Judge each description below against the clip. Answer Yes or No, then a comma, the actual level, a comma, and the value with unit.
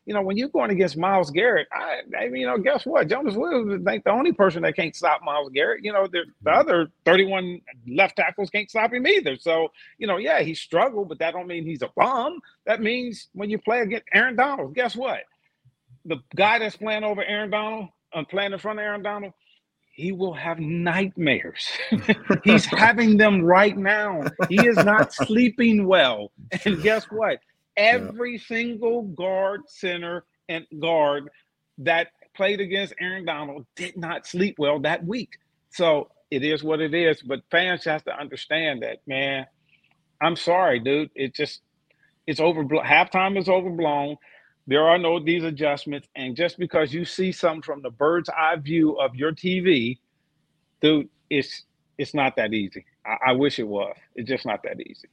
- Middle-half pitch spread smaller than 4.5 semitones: No, average, 4.8 semitones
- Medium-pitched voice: Yes, medium, 180 Hz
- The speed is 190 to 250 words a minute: No, average, 180 wpm